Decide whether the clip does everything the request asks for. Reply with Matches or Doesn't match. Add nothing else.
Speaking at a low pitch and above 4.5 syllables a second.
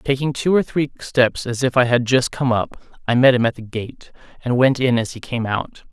Matches